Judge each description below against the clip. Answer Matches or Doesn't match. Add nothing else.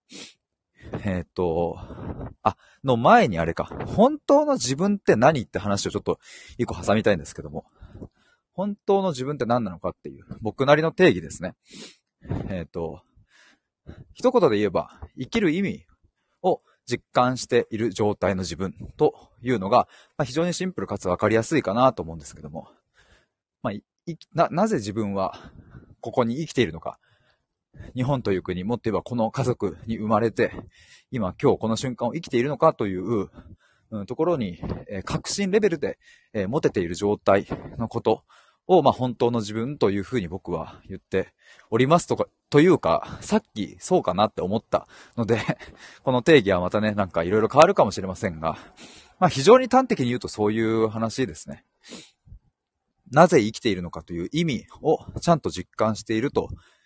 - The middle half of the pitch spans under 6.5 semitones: Doesn't match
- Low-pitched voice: Matches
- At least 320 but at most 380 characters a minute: Matches